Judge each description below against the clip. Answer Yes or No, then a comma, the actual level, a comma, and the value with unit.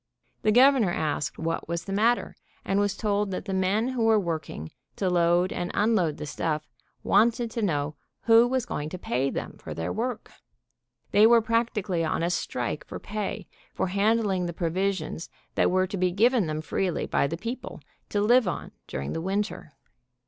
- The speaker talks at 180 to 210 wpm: Yes, average, 185 wpm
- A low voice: No, high, 195 Hz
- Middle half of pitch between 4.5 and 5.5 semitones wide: Yes, average, 4.9 semitones